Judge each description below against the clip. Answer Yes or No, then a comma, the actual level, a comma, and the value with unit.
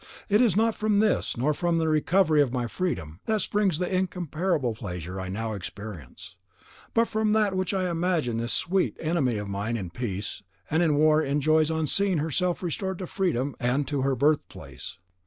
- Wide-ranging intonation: Yes, wide, 7.7 semitones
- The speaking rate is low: No, average, 190 wpm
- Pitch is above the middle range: No, medium, 155 Hz